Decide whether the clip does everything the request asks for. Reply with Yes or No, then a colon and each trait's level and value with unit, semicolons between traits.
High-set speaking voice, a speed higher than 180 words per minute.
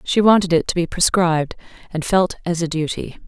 No: medium, 175 Hz; average, 200 wpm